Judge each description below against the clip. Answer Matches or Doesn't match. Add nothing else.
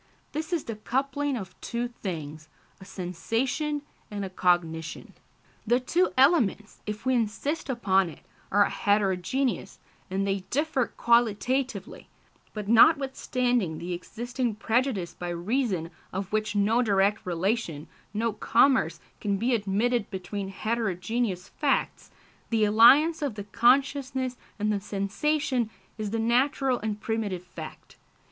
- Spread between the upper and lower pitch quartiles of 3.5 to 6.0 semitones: Matches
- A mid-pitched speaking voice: Doesn't match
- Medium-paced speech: Doesn't match